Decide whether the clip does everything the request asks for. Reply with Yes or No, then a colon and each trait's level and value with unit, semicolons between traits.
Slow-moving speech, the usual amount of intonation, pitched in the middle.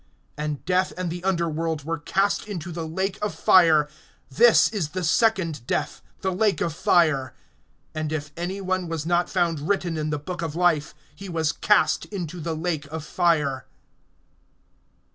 No: average, 165 wpm; average, 3.0 semitones; medium, 165 Hz